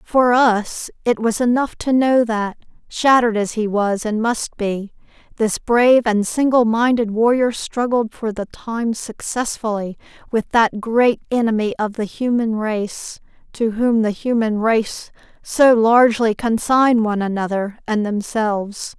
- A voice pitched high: Yes, high, 225 Hz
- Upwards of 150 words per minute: No, average, 145 wpm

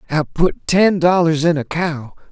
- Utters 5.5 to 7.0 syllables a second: No, 4.1 syllables/s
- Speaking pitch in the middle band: Yes, medium, 165 Hz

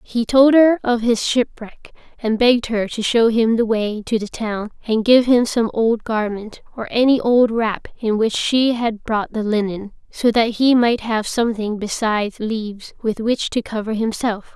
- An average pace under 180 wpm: No, average, 195 wpm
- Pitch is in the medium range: No, high, 225 Hz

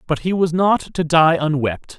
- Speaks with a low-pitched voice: No, medium, 160 Hz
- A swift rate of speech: Yes, fast, 210 wpm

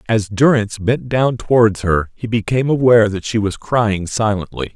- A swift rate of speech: No, average, 175 wpm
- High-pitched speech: No, low, 110 Hz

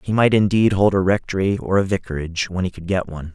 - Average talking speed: No, fast, 250 wpm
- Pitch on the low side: Yes, very low, 95 Hz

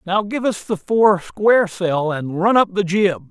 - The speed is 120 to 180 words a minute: No, average, 200 wpm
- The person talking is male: Yes, male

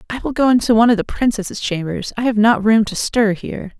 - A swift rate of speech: Yes, fast, 255 wpm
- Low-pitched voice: No, high, 220 Hz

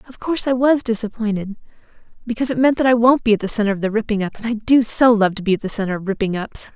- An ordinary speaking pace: No, fast, 265 wpm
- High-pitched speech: Yes, high, 225 Hz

